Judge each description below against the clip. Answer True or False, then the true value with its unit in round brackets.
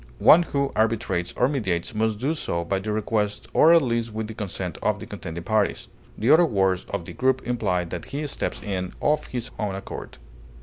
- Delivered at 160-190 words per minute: False (205 wpm)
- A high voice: False (110 Hz)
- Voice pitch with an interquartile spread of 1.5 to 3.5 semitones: False (5.3 semitones)